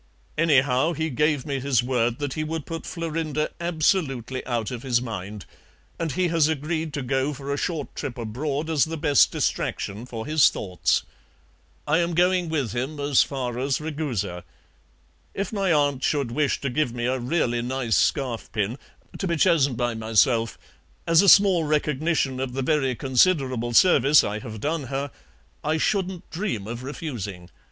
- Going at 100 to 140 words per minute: No, average, 170 wpm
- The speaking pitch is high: No, medium, 140 Hz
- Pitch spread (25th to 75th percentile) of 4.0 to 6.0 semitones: Yes, average, 4.6 semitones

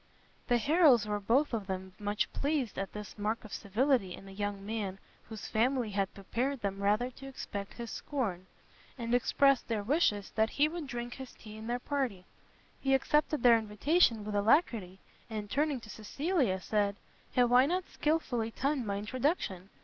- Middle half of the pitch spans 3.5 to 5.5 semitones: Yes, average, 4.8 semitones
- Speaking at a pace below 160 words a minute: No, average, 175 wpm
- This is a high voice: Yes, high, 230 Hz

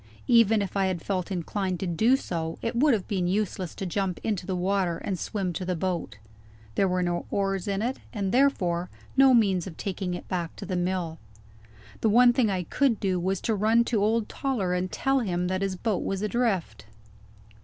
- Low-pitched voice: No, high, 195 Hz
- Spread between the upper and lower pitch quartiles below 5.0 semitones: Yes, average, 3.4 semitones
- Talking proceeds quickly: Yes, fast, 210 wpm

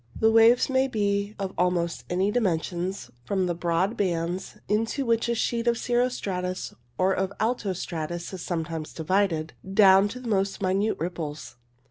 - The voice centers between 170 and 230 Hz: Yes, high, 190 Hz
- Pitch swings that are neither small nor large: Yes, average, 4.2 semitones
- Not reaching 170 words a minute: Yes, average, 160 wpm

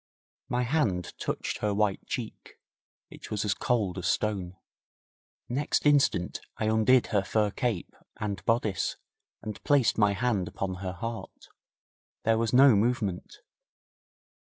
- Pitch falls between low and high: No, low, 110 Hz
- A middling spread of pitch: Yes, average, 3.7 semitones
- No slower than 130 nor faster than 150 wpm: Yes, slow, 135 wpm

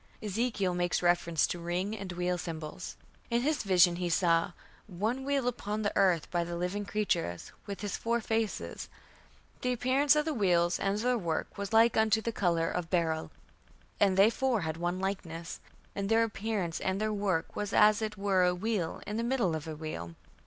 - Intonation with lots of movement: No, average, 4.1 semitones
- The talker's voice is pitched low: No, high, 195 Hz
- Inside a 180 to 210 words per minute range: Yes, average, 190 wpm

